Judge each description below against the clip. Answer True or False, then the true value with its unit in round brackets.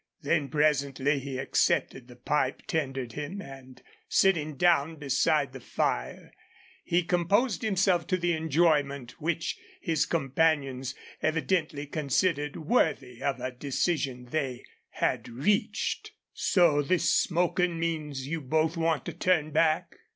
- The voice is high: False (150 Hz)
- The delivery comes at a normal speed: False (125 wpm)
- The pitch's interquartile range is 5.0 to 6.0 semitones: False (3.7 semitones)